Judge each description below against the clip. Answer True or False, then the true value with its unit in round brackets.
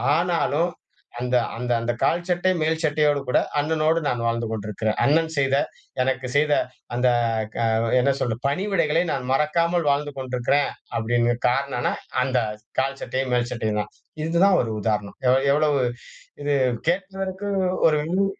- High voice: False (140 Hz)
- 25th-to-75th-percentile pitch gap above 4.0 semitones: True (4.9 semitones)